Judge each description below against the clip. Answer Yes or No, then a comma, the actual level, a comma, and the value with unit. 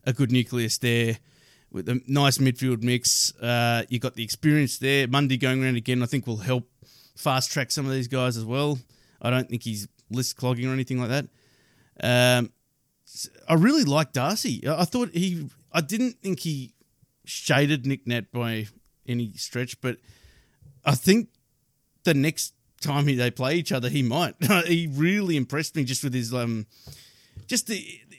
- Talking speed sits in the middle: Yes, average, 170 wpm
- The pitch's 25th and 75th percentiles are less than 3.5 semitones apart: Yes, average, 3.1 semitones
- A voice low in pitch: Yes, low, 130 Hz